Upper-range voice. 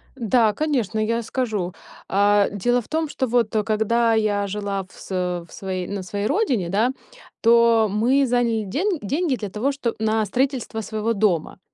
Yes: high, 220 Hz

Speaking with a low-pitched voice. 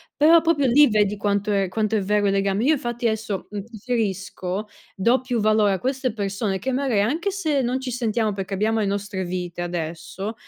No: high, 210 Hz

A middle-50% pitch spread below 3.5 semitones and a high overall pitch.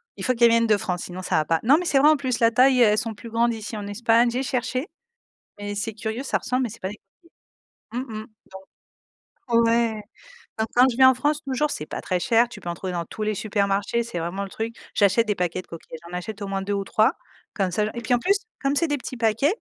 No: average, 3.8 semitones; high, 225 Hz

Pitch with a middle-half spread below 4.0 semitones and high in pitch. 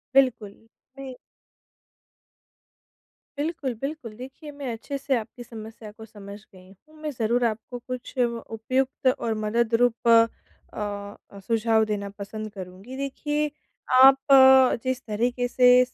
Yes: average, 3.4 semitones; high, 235 Hz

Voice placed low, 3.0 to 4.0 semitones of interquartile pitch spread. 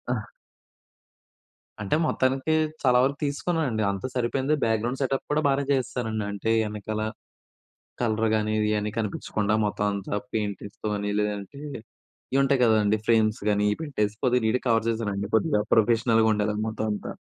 Yes: low, 110 Hz; average, 3.3 semitones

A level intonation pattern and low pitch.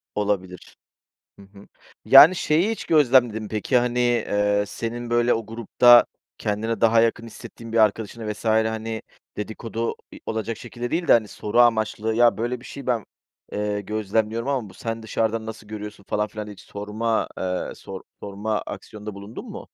Yes: narrow, 2.0 semitones; low, 110 Hz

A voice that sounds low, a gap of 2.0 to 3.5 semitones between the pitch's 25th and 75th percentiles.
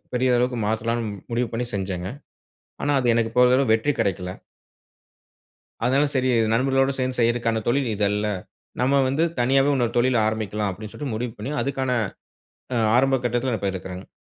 Yes: low, 120 Hz; average, 3.2 semitones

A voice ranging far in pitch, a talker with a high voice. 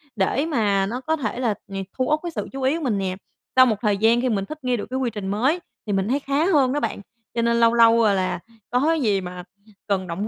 No: average, 4.8 semitones; high, 235 Hz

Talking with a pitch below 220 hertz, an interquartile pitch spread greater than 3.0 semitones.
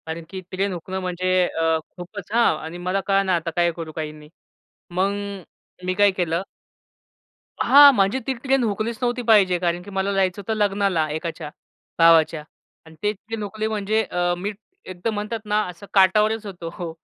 Yes: high, 190 Hz; average, 3.4 semitones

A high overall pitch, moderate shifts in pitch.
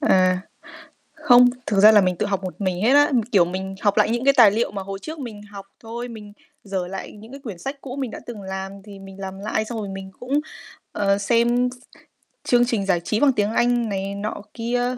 Yes: high, 210 Hz; average, 3.9 semitones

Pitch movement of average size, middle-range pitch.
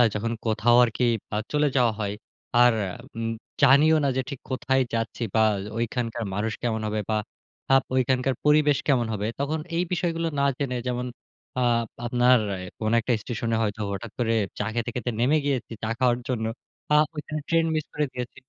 No: average, 3.6 semitones; low, 125 Hz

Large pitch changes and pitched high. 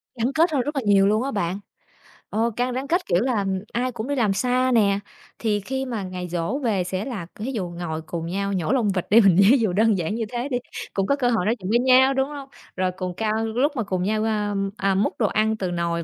No: average, 5.0 semitones; high, 220 Hz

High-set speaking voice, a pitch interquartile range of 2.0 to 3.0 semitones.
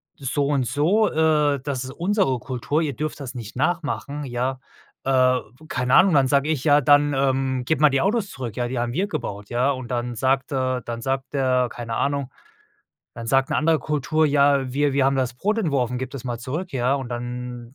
No: low, 135 Hz; average, 2.7 semitones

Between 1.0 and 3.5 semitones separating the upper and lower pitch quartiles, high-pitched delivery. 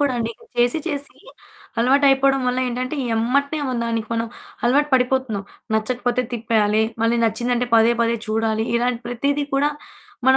Yes: average, 3.0 semitones; high, 245 Hz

